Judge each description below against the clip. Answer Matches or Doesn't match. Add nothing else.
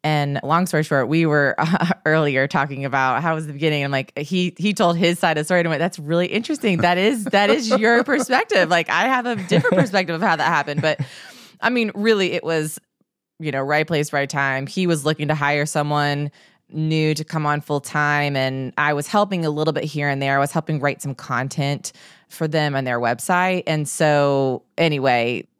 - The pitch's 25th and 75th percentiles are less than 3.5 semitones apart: Doesn't match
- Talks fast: Matches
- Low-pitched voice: Doesn't match